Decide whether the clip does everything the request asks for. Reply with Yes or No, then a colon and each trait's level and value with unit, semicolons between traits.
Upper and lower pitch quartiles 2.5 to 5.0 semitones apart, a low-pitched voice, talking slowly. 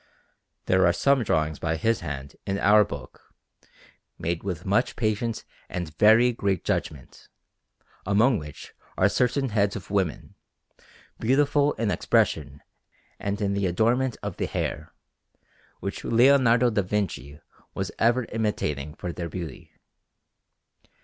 No: wide, 5.4 semitones; low, 100 Hz; slow, 130 wpm